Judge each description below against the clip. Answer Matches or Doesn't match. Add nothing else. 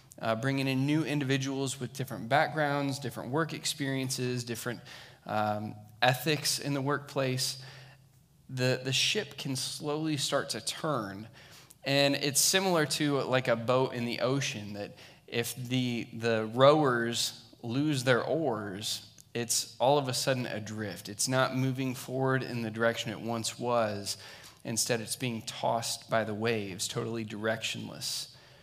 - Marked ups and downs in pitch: Doesn't match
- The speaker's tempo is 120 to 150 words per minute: Matches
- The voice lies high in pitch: Doesn't match